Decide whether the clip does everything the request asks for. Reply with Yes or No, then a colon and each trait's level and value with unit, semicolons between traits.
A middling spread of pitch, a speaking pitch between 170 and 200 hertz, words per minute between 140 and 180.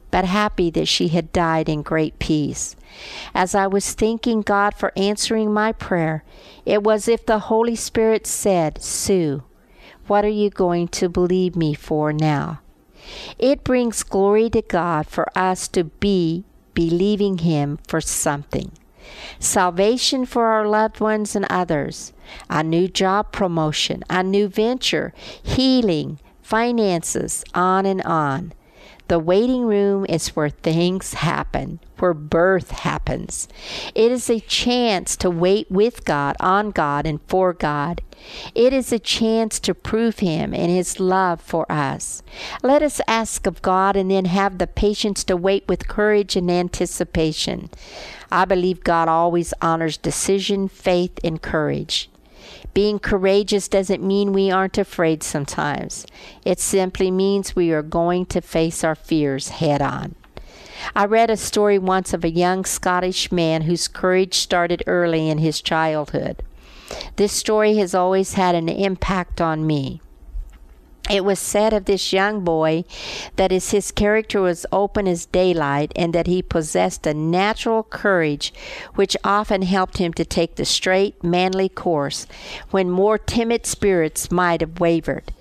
Yes: average, 3.6 semitones; medium, 185 Hz; average, 150 wpm